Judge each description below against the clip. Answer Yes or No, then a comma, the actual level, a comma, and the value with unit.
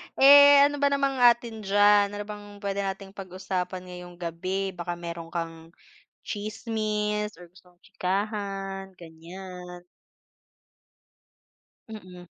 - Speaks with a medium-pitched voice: No, high, 195 Hz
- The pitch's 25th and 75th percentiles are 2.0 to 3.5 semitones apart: Yes, average, 2.9 semitones